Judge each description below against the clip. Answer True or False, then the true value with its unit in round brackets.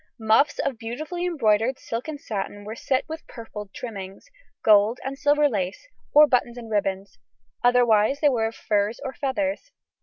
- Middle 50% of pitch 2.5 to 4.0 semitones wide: False (5.1 semitones)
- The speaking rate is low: False (160 wpm)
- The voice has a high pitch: True (235 Hz)